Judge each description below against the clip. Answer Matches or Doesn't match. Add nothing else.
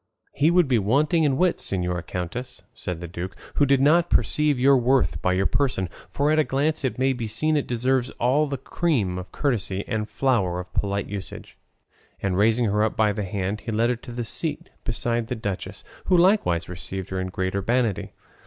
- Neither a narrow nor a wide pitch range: Doesn't match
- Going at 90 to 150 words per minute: Doesn't match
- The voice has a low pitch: Matches